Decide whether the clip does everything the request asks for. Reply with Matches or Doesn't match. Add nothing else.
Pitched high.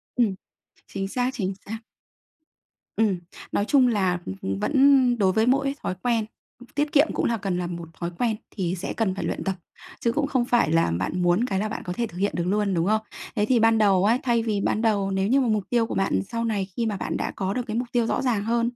Matches